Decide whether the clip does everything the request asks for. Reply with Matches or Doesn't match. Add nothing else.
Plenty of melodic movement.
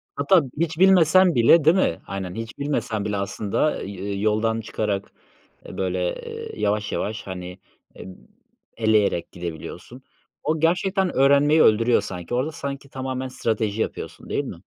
Matches